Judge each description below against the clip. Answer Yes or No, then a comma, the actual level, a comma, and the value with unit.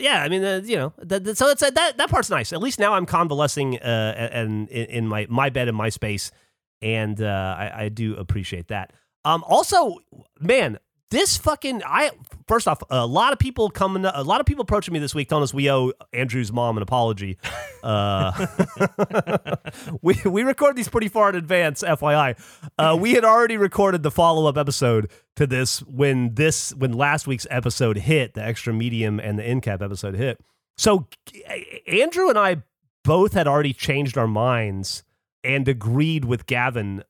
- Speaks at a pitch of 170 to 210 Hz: No, medium, 140 Hz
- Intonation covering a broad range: Yes, wide, 8.5 semitones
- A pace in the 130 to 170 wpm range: No, average, 190 wpm